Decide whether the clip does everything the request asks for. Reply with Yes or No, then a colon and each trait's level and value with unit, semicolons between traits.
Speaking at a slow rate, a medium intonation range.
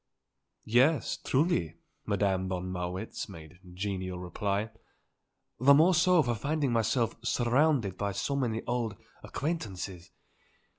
No: slow, 110 wpm; wide, 6.8 semitones